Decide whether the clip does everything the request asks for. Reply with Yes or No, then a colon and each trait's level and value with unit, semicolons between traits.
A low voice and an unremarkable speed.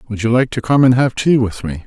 No: low, 120 Hz; fast, 320 wpm